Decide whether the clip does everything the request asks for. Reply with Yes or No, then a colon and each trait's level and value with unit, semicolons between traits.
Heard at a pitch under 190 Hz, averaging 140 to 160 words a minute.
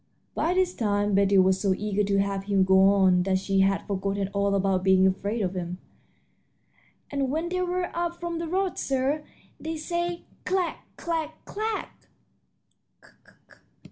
No: high, 205 Hz; average, 155 wpm